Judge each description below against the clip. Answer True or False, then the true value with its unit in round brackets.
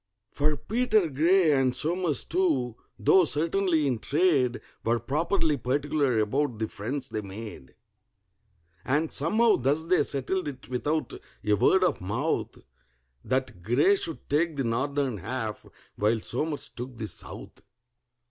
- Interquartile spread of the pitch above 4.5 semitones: True (5.2 semitones)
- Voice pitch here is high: False (140 Hz)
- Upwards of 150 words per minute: False (135 wpm)